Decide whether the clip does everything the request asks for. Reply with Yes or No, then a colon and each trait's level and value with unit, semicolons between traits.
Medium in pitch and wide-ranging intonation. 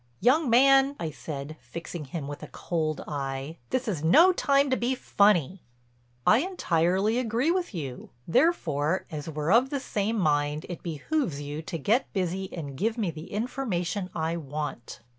Yes: medium, 175 Hz; wide, 7.8 semitones